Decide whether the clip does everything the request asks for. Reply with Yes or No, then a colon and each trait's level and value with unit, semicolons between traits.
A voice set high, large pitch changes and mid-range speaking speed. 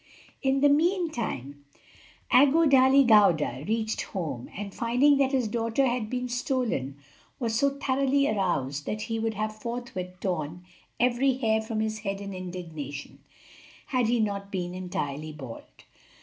Yes: high, 220 Hz; wide, 5.9 semitones; average, 150 wpm